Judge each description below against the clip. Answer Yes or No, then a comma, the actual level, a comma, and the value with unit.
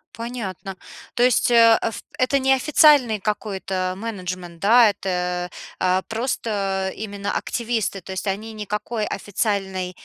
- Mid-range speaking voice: No, high, 210 Hz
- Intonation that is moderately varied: Yes, average, 3.6 semitones